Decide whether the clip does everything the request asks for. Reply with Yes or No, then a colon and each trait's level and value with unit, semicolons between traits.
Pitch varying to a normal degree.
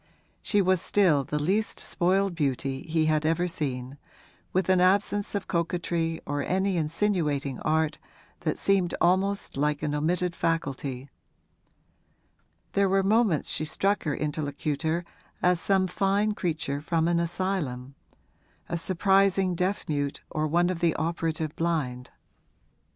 Yes: average, 3.9 semitones